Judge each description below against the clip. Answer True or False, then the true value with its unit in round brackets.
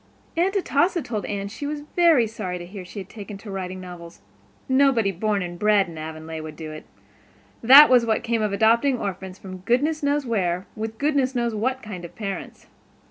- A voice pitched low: False (215 Hz)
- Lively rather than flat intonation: True (5.7 semitones)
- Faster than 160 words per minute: True (195 wpm)